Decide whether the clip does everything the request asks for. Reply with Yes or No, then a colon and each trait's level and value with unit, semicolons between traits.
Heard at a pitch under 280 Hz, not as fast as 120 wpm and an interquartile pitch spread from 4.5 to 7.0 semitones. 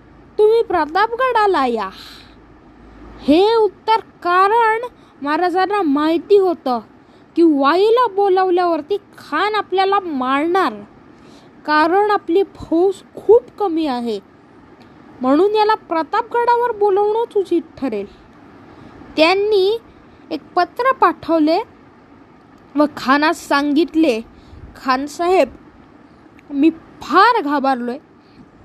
No: very high, 345 Hz; slow, 80 wpm; wide, 5.6 semitones